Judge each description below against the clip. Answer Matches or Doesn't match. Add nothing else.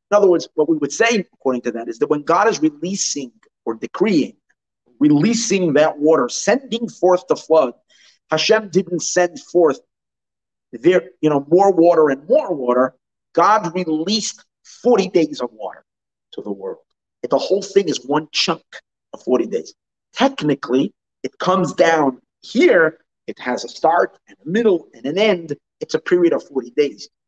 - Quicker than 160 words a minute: Matches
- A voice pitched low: Doesn't match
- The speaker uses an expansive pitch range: Matches